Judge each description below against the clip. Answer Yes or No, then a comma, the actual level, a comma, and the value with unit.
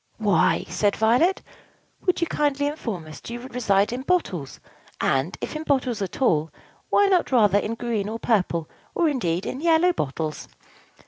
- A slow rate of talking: No, average, 170 wpm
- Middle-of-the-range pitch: No, high, 230 Hz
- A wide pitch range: Yes, wide, 7.0 semitones